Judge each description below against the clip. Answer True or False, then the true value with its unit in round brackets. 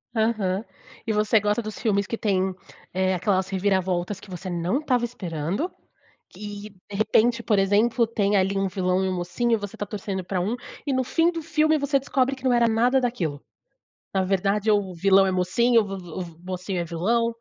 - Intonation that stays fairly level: False (3.9 semitones)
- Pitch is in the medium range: False (205 Hz)